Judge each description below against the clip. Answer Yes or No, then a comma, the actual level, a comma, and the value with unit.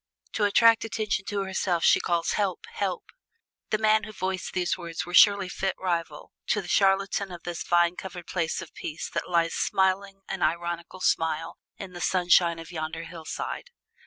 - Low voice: No, medium, 180 Hz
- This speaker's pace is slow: No, average, 175 wpm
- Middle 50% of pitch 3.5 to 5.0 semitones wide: No, narrow, 2.5 semitones